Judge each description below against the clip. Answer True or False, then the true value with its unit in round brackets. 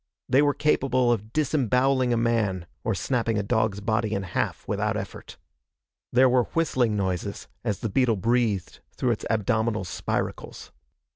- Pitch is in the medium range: False (115 Hz)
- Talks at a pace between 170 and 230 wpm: False (150 wpm)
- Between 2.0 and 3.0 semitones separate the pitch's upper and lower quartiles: False (3.4 semitones)